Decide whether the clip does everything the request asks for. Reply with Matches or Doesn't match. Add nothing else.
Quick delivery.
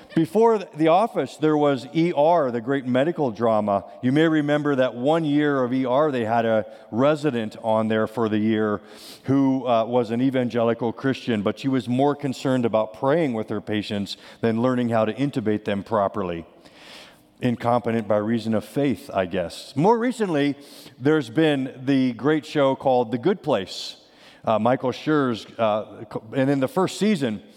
Doesn't match